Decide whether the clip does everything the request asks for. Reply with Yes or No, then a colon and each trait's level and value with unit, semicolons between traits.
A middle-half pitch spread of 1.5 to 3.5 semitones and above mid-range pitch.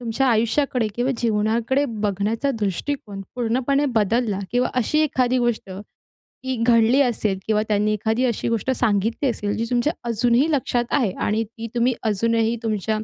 Yes: average, 2.8 semitones; high, 230 Hz